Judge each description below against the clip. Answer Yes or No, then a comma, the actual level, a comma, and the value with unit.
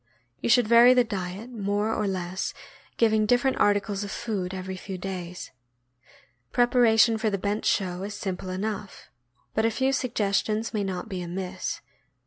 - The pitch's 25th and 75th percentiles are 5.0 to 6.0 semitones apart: No, average, 3.1 semitones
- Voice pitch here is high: Yes, high, 205 Hz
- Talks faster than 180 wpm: No, average, 155 wpm